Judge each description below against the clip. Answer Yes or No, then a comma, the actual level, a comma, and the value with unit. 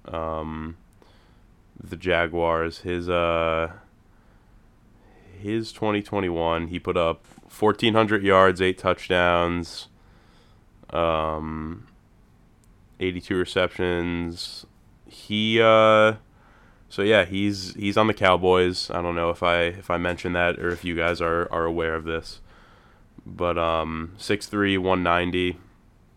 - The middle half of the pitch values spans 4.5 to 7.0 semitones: No, average, 3.2 semitones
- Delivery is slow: Yes, slow, 115 wpm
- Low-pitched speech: Yes, very low, 90 Hz